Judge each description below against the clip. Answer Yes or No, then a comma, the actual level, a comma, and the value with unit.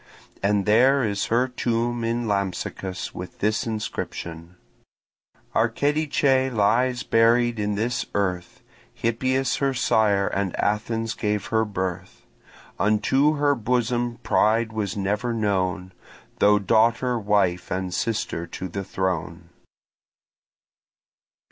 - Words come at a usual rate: No, slow, 110 wpm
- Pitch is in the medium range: No, low, 110 Hz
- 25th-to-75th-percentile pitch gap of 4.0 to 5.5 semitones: No, average, 3.5 semitones